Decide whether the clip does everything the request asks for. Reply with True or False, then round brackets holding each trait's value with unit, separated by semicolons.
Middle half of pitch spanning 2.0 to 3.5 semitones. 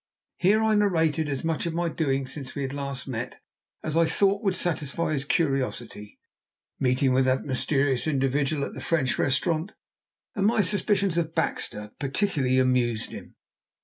False (4.3 semitones)